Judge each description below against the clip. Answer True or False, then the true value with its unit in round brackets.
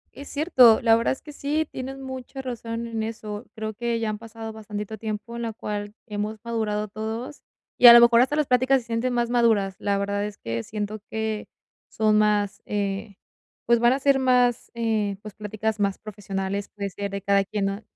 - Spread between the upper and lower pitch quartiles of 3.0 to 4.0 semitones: False (2.5 semitones)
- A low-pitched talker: False (220 Hz)